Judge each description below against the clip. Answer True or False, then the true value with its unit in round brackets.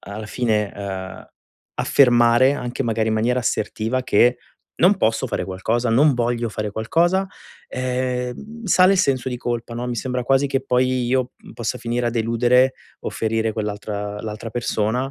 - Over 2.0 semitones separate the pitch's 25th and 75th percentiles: True (2.6 semitones)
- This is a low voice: True (120 Hz)